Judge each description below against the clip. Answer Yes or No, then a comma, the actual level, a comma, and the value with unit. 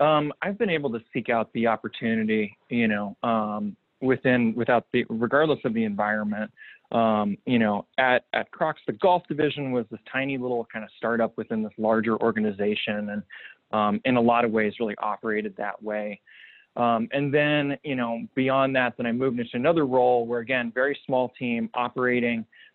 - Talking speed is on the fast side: No, average, 180 wpm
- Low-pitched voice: Yes, low, 115 Hz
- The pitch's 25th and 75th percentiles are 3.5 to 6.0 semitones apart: No, average, 2.9 semitones